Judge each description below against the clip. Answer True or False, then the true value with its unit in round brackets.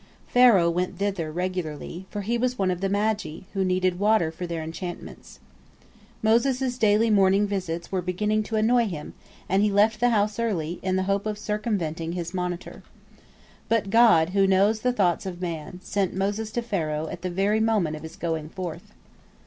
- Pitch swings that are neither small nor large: True (3.6 semitones)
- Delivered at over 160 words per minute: True (180 wpm)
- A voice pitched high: True (195 Hz)